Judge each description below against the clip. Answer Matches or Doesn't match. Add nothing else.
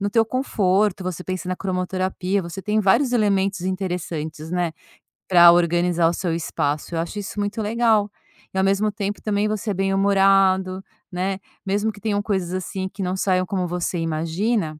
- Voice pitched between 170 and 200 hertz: Matches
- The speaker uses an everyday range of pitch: Doesn't match